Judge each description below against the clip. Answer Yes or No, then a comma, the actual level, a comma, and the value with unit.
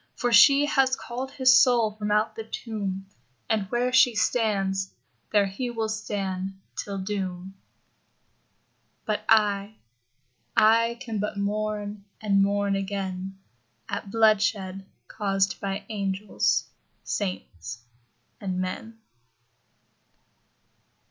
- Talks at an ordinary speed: No, slow, 105 wpm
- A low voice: No, high, 205 Hz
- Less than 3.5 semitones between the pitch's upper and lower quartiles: Yes, narrow, 2.4 semitones